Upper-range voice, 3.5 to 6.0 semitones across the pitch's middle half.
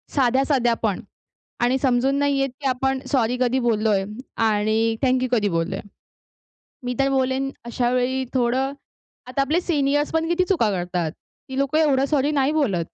No: very high, 260 Hz; average, 3.1 semitones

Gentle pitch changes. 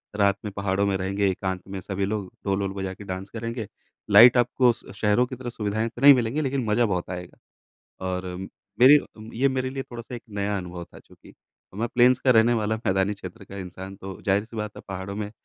No: average, 3.7 semitones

